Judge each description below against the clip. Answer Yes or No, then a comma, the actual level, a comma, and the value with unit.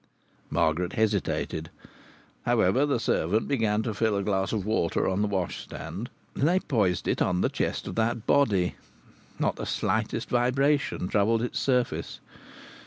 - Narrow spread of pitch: No, average, 4.2 semitones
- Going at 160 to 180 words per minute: No, average, 150 wpm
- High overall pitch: No, low, 110 Hz